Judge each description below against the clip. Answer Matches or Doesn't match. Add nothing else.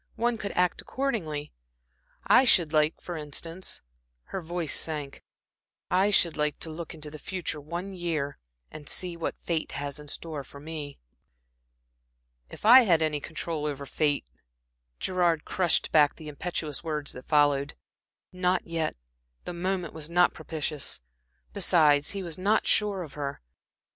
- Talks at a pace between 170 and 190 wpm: Doesn't match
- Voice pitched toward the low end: Doesn't match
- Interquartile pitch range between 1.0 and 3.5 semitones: Matches